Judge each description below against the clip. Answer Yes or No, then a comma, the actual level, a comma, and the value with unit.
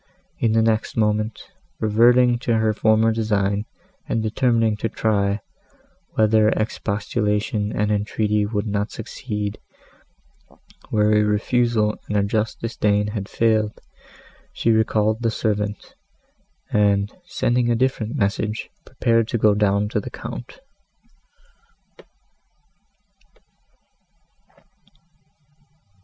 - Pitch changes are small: Yes, narrow, 1.5 semitones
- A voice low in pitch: Yes, low, 110 Hz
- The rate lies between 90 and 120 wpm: Yes, slow, 105 wpm